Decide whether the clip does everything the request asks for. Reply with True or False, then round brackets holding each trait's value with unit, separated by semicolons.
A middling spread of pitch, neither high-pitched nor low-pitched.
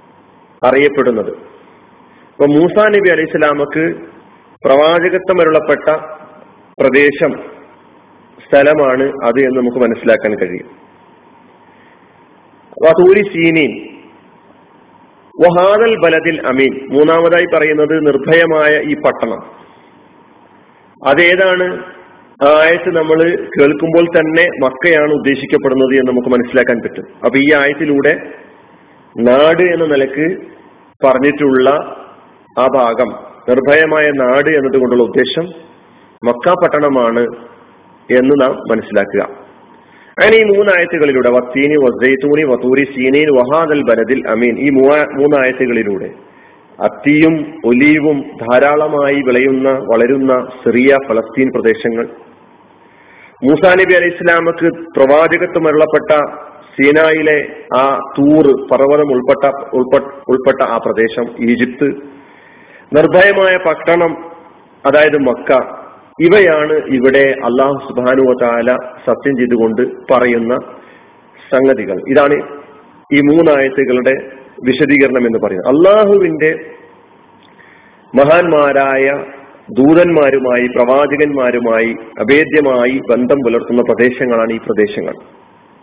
True (3.5 semitones; 145 Hz)